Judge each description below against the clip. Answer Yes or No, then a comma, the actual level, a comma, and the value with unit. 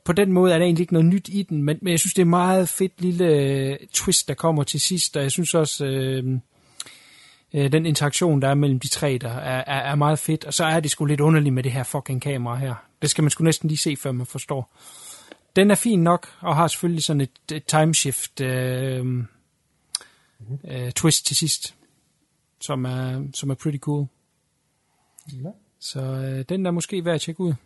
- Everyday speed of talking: Yes, average, 205 wpm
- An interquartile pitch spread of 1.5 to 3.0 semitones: No, average, 3.8 semitones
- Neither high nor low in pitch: Yes, medium, 150 Hz